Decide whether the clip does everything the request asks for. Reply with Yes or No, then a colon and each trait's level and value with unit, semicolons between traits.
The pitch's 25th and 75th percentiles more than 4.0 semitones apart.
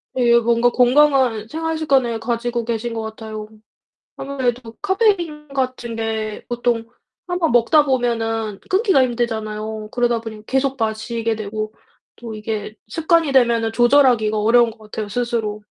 No: average, 2.9 semitones